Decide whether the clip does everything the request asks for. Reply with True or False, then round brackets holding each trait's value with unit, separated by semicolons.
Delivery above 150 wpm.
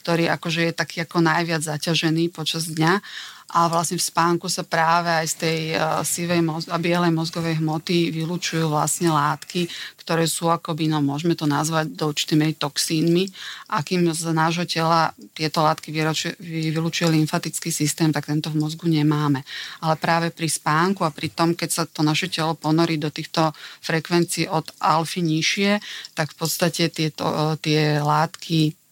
True (160 wpm)